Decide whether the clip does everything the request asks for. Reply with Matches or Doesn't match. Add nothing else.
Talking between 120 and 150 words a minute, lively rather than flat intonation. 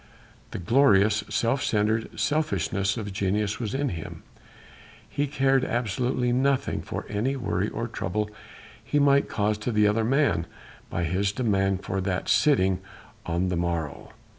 Doesn't match